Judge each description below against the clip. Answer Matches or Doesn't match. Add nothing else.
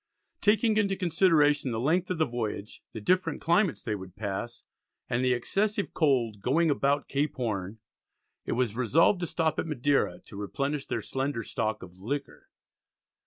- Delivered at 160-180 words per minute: Matches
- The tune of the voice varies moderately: Doesn't match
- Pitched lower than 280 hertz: Matches